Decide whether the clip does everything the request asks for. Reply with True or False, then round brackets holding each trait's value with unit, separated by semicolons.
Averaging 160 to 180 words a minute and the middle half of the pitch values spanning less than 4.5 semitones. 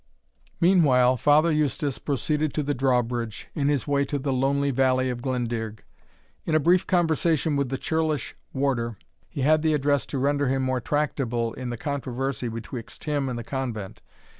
True (170 wpm; 3.0 semitones)